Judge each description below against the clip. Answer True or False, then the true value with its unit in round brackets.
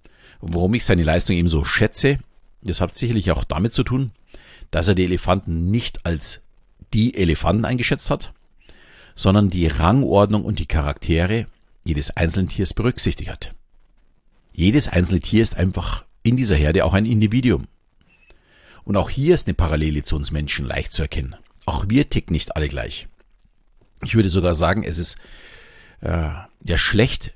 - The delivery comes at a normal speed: True (160 wpm)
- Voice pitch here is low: True (90 Hz)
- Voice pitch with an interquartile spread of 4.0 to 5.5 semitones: True (4.9 semitones)